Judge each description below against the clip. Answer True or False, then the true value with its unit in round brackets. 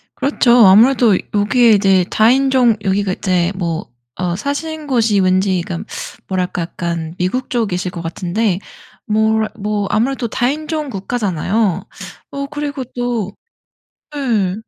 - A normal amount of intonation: True (5.0 semitones)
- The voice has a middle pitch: False (210 Hz)